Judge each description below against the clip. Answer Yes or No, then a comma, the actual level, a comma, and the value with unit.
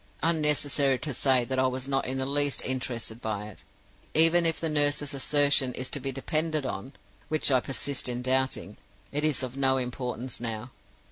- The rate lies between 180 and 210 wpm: Yes, average, 185 wpm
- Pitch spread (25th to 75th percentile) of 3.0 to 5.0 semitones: No, narrow, 2.5 semitones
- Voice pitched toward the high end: No, low, 135 Hz